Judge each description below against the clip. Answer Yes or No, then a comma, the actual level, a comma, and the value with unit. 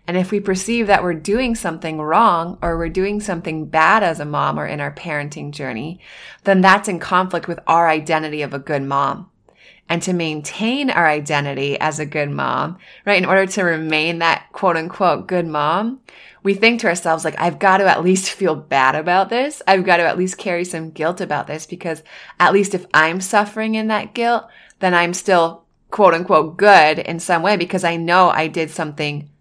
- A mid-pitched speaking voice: Yes, medium, 170 Hz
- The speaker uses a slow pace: No, fast, 205 wpm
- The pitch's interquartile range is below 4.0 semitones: Yes, average, 3.5 semitones